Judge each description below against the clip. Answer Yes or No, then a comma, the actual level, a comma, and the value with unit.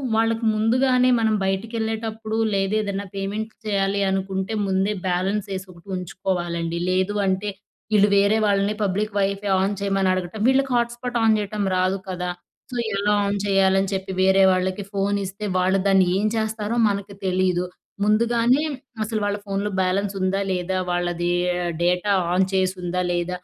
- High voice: Yes, high, 195 Hz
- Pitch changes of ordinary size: No, narrow, 2.2 semitones